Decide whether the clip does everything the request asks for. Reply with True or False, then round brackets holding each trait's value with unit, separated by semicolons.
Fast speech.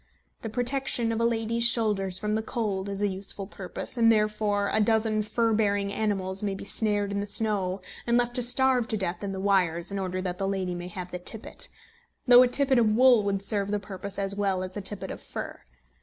True (225 wpm)